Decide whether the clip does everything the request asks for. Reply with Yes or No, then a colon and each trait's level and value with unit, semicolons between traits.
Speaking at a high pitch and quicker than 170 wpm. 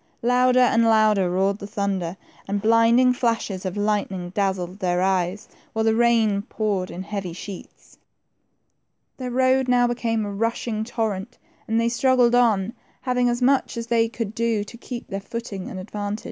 No: high, 220 Hz; average, 165 wpm